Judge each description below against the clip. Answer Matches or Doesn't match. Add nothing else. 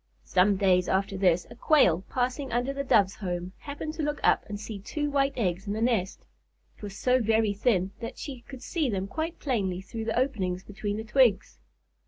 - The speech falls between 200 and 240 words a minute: Matches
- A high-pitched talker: Matches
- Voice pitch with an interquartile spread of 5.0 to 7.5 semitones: Matches